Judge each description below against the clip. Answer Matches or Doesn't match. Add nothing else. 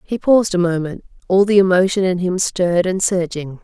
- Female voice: Matches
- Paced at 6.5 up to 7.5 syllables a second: Doesn't match